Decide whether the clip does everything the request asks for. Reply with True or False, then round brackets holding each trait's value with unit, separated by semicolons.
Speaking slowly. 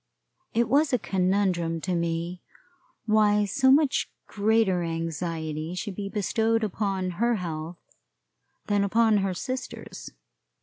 True (120 wpm)